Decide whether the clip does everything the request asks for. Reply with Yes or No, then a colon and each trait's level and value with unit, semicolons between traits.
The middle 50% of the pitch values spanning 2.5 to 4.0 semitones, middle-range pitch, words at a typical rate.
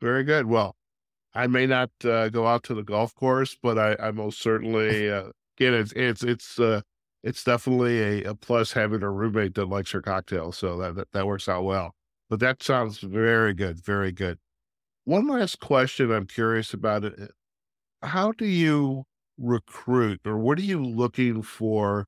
No: average, 3.5 semitones; low, 110 Hz; average, 180 wpm